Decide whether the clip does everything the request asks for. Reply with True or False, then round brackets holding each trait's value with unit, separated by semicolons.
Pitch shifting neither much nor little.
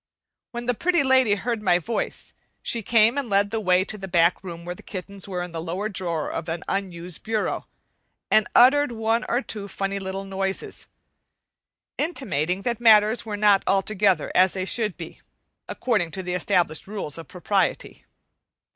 True (3.7 semitones)